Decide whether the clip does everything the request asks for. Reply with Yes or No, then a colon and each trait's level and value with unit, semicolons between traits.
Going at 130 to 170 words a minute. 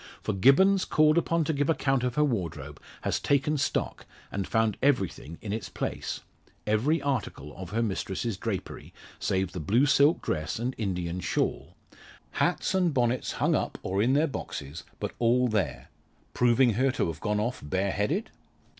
Yes: average, 165 wpm